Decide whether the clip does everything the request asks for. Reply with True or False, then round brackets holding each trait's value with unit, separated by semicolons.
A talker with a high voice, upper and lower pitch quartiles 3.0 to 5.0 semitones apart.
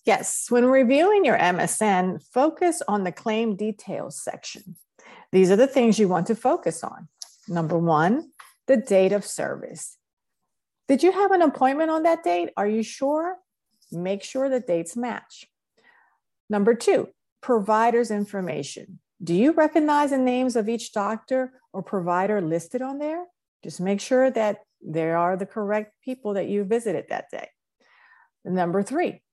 False (220 Hz; 5.5 semitones)